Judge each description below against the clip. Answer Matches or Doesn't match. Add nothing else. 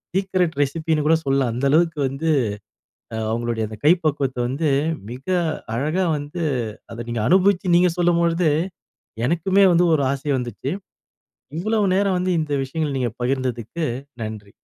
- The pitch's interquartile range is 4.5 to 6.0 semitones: Matches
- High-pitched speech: Doesn't match